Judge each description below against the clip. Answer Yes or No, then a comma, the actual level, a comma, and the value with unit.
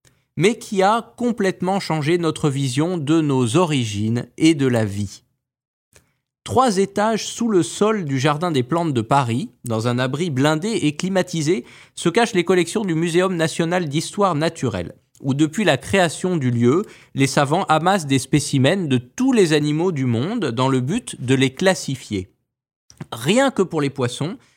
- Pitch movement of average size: No, wide, 5.8 semitones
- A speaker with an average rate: Yes, average, 165 wpm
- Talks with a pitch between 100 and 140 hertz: No, medium, 160 Hz